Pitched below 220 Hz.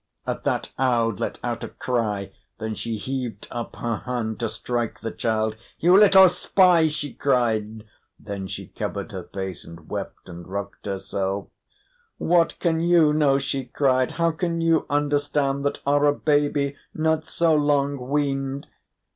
Yes: low, 135 Hz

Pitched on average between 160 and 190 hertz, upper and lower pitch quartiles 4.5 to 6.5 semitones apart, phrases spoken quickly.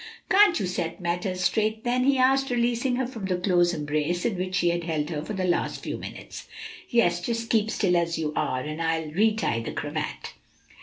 Yes: medium, 185 Hz; wide, 5.6 semitones; fast, 210 wpm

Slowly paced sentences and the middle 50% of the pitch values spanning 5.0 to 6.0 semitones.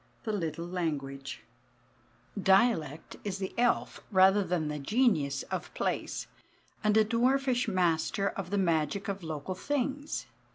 Yes: slow, 130 wpm; average, 5.3 semitones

